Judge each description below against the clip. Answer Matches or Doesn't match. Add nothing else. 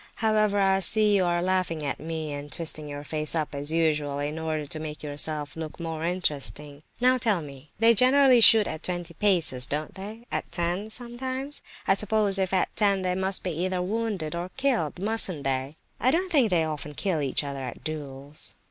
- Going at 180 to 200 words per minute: Matches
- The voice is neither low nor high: Matches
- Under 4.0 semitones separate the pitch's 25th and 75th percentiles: Doesn't match